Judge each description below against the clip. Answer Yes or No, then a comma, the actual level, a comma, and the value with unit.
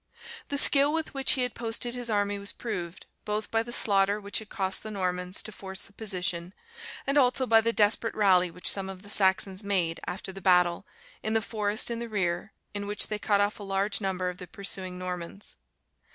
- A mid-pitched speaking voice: No, high, 200 Hz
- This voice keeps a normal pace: No, fast, 210 wpm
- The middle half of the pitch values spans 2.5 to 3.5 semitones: Yes, average, 3.0 semitones